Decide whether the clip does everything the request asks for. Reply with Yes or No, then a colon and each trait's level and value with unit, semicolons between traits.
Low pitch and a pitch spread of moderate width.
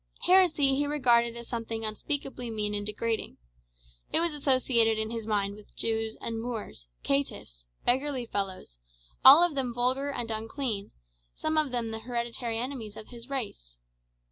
No: high, 235 Hz; average, 3.6 semitones